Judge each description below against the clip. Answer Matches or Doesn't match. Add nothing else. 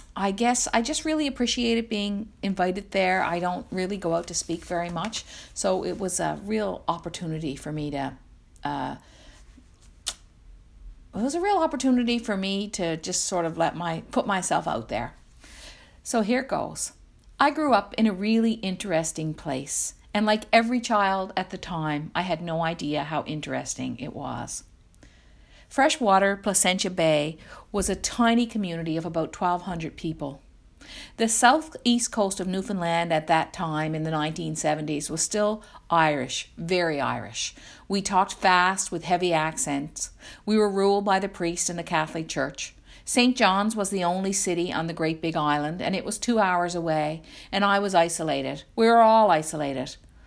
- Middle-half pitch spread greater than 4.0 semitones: Matches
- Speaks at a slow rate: Doesn't match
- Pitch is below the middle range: Doesn't match